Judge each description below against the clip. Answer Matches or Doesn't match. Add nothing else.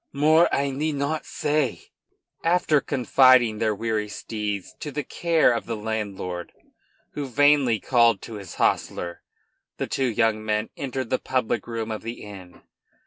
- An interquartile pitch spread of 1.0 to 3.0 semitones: Doesn't match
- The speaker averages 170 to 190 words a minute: Doesn't match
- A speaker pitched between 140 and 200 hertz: Doesn't match